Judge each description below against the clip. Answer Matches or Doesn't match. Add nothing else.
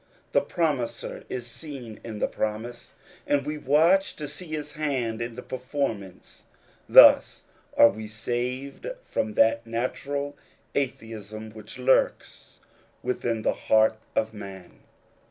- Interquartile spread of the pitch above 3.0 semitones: Matches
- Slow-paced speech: Matches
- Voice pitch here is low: Matches